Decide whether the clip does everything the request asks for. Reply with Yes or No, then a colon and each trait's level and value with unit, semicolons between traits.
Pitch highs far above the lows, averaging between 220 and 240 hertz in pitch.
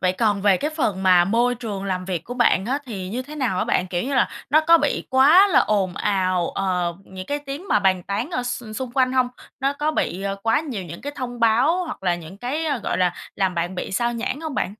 Yes: wide, 6.4 semitones; high, 225 Hz